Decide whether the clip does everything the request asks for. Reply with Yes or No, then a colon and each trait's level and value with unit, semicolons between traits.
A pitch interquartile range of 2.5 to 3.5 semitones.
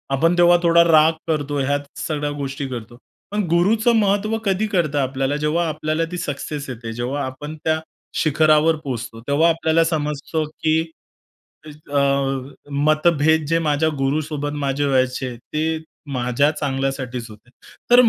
Yes: average, 3.1 semitones